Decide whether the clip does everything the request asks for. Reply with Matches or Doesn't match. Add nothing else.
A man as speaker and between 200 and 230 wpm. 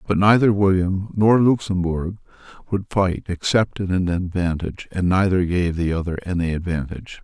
Doesn't match